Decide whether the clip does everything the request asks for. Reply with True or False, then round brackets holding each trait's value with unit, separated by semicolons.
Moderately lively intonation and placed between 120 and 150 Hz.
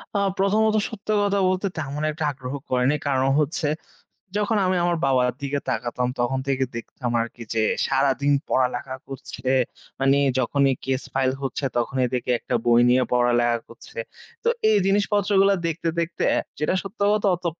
False (6.7 semitones; 135 Hz)